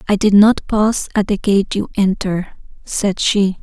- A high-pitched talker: Yes, high, 200 Hz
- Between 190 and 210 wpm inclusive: No, average, 180 wpm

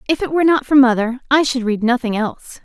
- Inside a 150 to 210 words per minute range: No, fast, 250 wpm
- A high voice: Yes, very high, 255 Hz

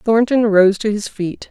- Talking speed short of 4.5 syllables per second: Yes, 4.1 syllables/s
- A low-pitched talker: No, high, 210 Hz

